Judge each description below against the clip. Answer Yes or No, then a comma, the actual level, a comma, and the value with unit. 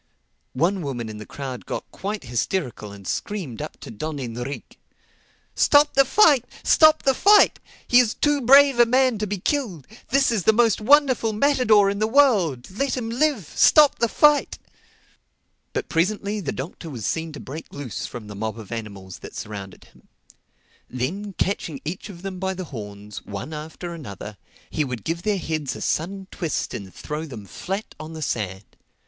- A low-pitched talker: No, medium, 175 Hz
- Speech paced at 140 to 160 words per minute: No, average, 180 wpm